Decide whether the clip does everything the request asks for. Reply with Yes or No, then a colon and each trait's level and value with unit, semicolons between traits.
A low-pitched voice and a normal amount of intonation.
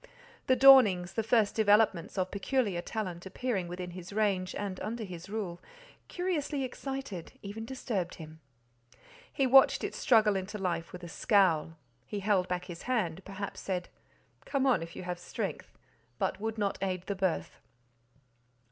No: high, 200 Hz; average, 3.8 semitones